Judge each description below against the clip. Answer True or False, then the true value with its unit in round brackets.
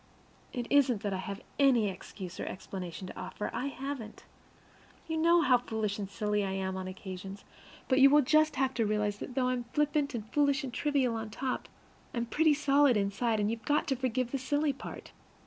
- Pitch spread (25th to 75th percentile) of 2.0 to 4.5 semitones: False (5.3 semitones)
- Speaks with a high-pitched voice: True (245 Hz)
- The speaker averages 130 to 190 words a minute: False (205 wpm)